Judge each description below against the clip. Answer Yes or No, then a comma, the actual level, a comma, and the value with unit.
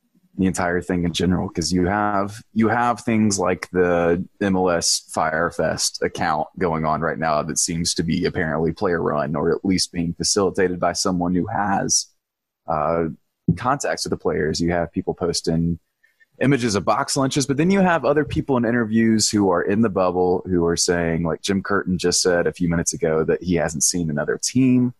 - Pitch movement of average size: Yes, average, 4.8 semitones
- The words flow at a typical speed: Yes, average, 190 wpm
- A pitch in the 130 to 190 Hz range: No, very low, 90 Hz